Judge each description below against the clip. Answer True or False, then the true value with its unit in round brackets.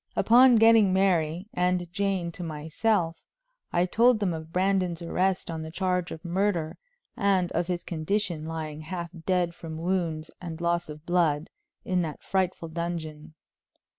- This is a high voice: False (175 Hz)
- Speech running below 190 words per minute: True (150 wpm)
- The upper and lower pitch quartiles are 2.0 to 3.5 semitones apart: True (2.6 semitones)